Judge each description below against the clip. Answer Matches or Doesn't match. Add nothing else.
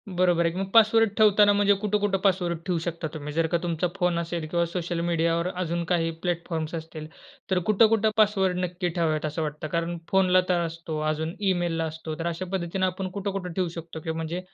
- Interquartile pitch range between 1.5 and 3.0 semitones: Matches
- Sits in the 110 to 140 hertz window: Doesn't match